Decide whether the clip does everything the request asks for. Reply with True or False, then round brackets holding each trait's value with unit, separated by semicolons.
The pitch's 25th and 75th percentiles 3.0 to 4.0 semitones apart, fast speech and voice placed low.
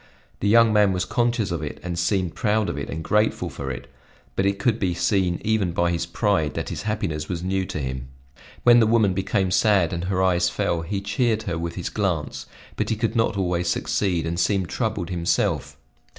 True (3.7 semitones; 210 wpm; 95 Hz)